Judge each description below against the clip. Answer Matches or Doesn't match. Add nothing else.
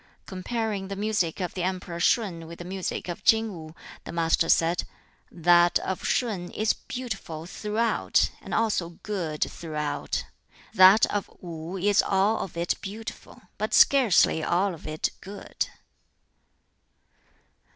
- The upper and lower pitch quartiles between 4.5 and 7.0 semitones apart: Doesn't match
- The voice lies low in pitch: Doesn't match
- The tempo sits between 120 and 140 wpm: Matches